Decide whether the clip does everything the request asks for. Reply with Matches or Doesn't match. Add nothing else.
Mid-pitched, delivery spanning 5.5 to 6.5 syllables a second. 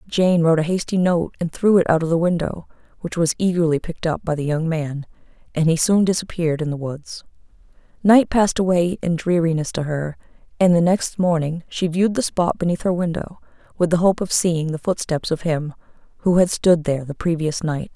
Matches